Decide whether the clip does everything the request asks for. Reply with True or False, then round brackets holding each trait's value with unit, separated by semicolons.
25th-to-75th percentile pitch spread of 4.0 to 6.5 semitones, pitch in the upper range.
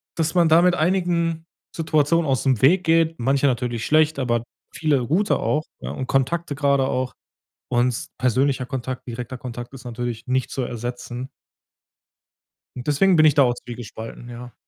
False (4.3 semitones; 135 Hz)